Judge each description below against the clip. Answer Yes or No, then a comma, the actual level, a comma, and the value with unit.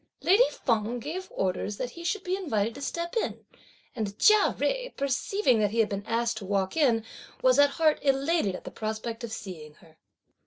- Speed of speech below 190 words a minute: No, average, 195 wpm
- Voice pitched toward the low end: No, high, 235 Hz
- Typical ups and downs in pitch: No, wide, 7.8 semitones